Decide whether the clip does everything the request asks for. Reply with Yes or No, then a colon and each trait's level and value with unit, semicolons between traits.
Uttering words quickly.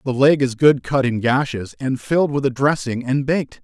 Yes: fast, 230 wpm